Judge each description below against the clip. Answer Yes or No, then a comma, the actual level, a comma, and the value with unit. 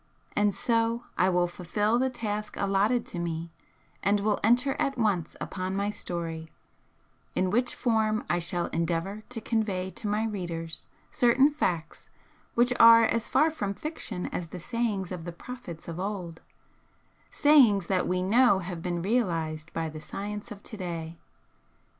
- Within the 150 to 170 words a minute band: Yes, average, 160 wpm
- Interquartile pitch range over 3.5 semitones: Yes, average, 4.8 semitones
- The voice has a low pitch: No, high, 200 Hz